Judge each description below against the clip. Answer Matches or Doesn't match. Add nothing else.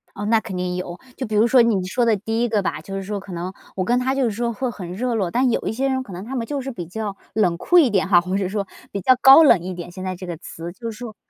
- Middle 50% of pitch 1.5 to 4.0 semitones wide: Doesn't match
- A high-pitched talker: Matches